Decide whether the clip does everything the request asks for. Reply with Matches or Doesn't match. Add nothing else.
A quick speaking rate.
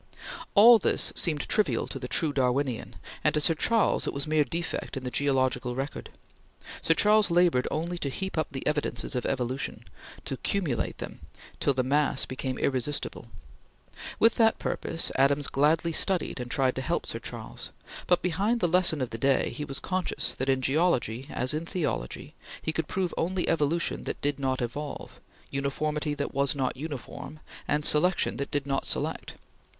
Doesn't match